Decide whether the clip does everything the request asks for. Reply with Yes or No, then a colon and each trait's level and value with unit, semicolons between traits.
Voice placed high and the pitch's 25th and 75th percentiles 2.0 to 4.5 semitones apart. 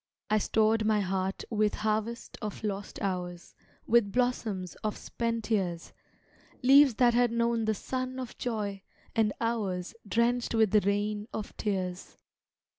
Yes: high, 215 Hz; average, 2.7 semitones